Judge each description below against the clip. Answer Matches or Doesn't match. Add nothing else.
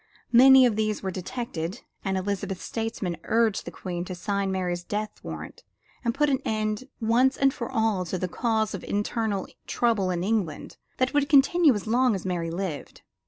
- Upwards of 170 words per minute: Matches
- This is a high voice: Matches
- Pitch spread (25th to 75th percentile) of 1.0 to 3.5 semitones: Doesn't match